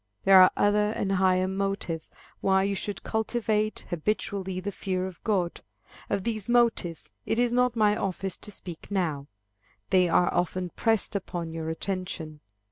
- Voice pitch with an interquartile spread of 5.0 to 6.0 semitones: No, average, 2.7 semitones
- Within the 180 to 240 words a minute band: No, average, 155 wpm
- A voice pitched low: No, high, 195 Hz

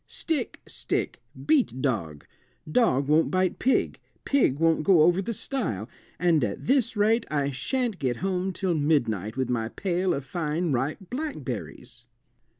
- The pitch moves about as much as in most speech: No, wide, 7.1 semitones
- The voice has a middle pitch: Yes, medium, 165 Hz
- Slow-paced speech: No, average, 150 wpm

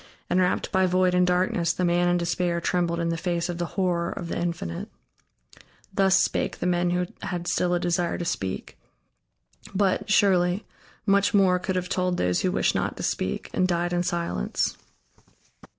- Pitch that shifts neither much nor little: No, narrow, 1.2 semitones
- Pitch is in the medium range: Yes, medium, 180 Hz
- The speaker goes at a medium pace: Yes, average, 180 wpm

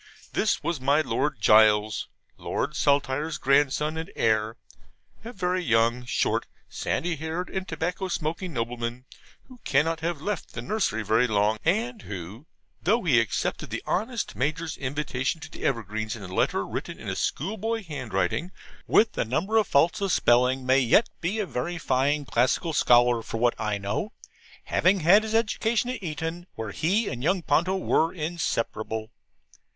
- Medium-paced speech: Yes, average, 165 wpm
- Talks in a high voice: No, medium, 150 Hz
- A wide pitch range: Yes, wide, 7.1 semitones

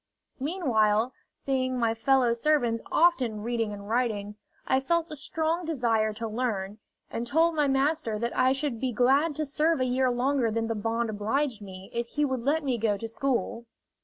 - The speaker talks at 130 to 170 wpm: No, average, 185 wpm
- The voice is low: No, high, 245 Hz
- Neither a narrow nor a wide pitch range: Yes, average, 3.8 semitones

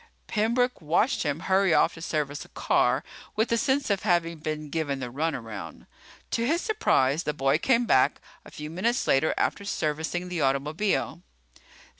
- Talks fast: No, average, 165 wpm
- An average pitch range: No, wide, 6.3 semitones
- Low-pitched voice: No, medium, 165 Hz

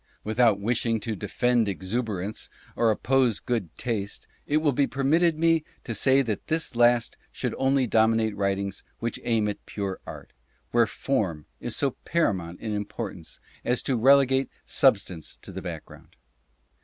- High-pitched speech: No, low, 115 Hz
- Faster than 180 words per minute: No, average, 155 wpm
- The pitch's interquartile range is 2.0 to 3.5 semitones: No, average, 4.5 semitones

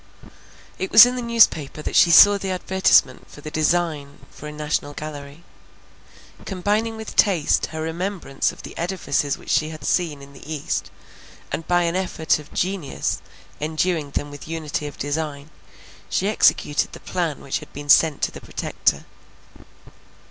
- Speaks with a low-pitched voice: No, medium, 160 Hz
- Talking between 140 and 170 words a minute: Yes, average, 165 wpm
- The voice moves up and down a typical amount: Yes, average, 4.0 semitones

